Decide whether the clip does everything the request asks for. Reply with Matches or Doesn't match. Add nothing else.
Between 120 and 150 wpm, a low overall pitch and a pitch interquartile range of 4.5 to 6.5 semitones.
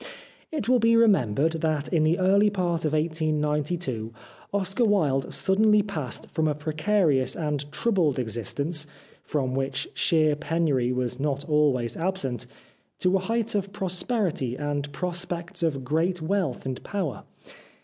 Doesn't match